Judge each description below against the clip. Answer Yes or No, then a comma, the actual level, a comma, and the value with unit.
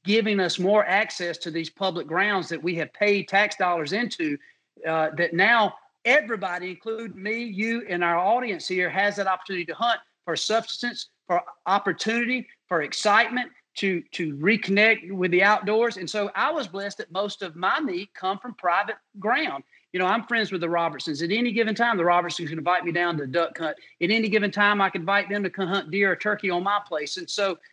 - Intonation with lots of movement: No, average, 3.7 semitones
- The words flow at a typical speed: No, fast, 210 wpm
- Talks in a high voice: Yes, high, 195 Hz